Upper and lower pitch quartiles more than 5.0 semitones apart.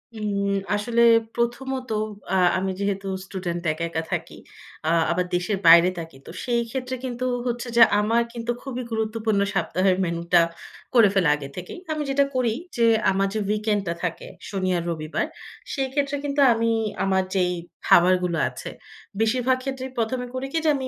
Yes: wide, 5.5 semitones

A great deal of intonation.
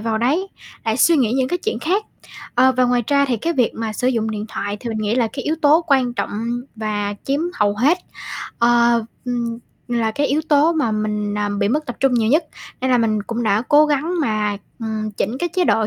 No: average, 4.7 semitones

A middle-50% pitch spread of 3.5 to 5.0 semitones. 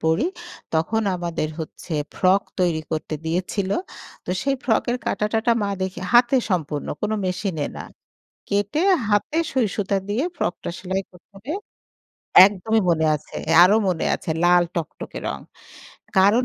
Yes: average, 3.8 semitones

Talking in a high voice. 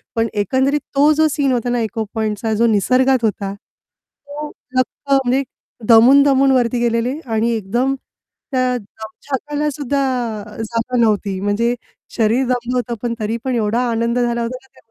Yes: high, 240 Hz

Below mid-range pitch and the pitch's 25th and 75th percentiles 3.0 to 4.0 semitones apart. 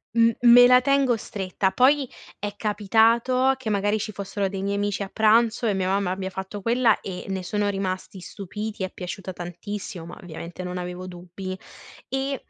No: high, 200 Hz; average, 3.5 semitones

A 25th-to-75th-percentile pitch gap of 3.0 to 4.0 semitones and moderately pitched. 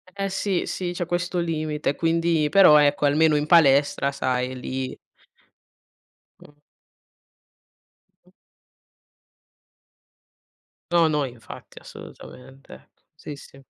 Yes: average, 3.6 semitones; medium, 150 Hz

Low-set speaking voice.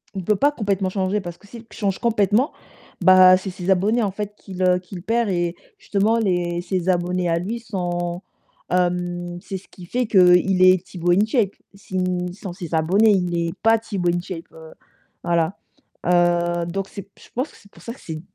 No: medium, 185 Hz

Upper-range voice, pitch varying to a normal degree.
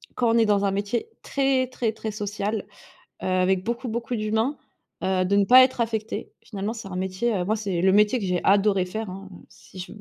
Yes: high, 210 Hz; average, 3.1 semitones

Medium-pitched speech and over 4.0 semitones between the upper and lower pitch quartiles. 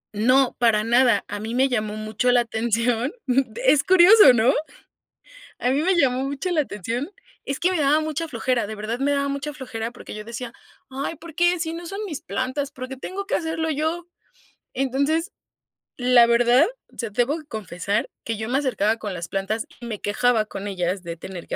No: very high, 250 Hz; average, 5.1 semitones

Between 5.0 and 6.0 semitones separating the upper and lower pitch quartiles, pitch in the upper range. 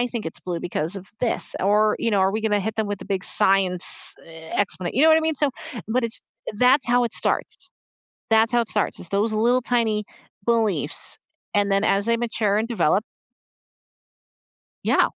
No: average, 2.9 semitones; high, 215 Hz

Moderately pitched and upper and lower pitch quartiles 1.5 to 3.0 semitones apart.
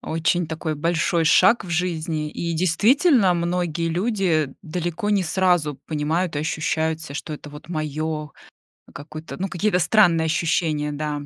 Yes: medium, 165 Hz; narrow, 2.5 semitones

